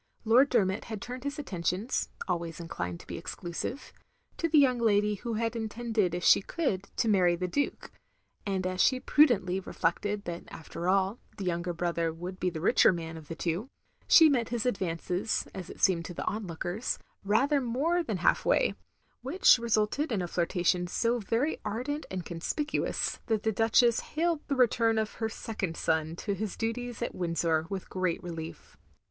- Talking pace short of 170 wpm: No, average, 185 wpm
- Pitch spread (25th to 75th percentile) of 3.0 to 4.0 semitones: No, average, 5.3 semitones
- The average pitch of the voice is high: Yes, high, 205 Hz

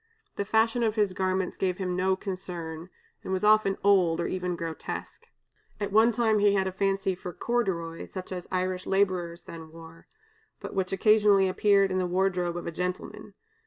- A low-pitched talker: No, medium, 185 Hz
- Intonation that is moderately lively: No, narrow, 2.0 semitones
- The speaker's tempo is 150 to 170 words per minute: No, average, 180 wpm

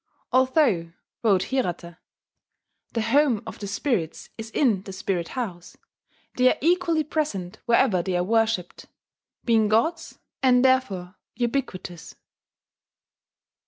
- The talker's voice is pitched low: No, high, 225 Hz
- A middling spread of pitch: No, wide, 6.0 semitones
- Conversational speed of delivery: No, slow, 115 wpm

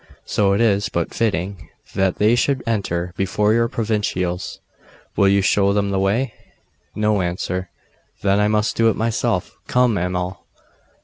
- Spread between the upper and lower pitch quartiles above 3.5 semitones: No, average, 2.8 semitones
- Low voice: Yes, low, 100 Hz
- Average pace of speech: Yes, average, 150 wpm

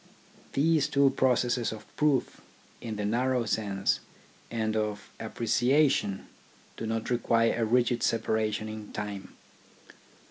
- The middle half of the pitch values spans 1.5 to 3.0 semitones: Yes, narrow, 2.6 semitones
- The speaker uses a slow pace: Yes, slow, 115 wpm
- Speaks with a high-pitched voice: No, low, 115 Hz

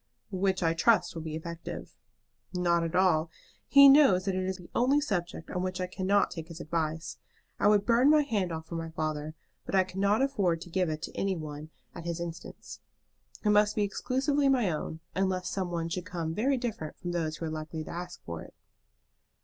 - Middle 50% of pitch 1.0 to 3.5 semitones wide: No, average, 3.9 semitones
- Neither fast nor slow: No, fast, 210 wpm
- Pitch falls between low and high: Yes, medium, 180 Hz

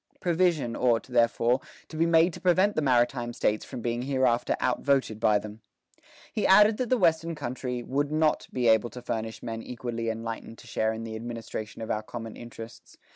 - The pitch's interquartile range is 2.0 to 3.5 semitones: No, average, 5.0 semitones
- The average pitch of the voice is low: Yes, low, 120 Hz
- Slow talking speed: No, average, 185 wpm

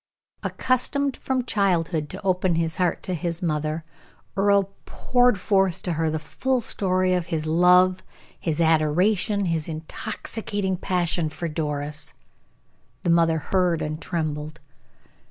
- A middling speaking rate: No, slow, 130 wpm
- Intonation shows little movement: No, average, 3.3 semitones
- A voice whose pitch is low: No, medium, 175 Hz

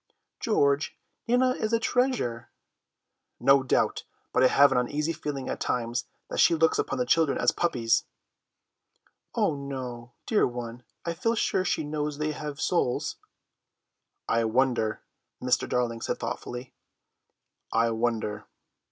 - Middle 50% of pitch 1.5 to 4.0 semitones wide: No, average, 4.7 semitones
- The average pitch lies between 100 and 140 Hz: Yes, low, 135 Hz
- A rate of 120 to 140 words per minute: Yes, slow, 135 wpm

